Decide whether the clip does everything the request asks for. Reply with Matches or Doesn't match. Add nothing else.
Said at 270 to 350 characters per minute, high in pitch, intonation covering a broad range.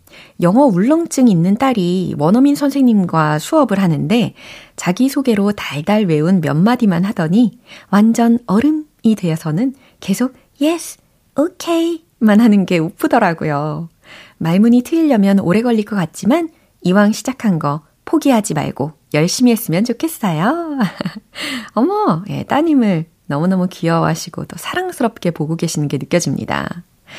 Matches